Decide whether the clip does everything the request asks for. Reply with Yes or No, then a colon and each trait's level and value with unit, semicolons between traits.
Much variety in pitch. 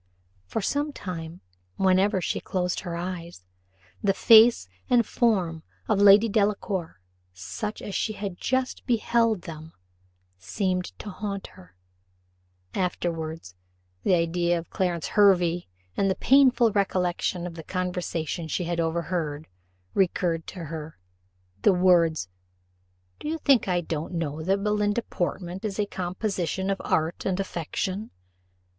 No: average, 3.4 semitones